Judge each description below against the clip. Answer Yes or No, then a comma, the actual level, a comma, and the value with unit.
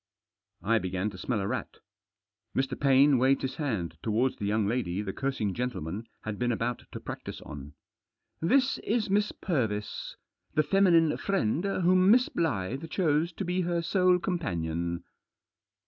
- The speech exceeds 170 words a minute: No, average, 150 wpm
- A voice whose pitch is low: Yes, low, 130 Hz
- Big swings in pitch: Yes, wide, 8.8 semitones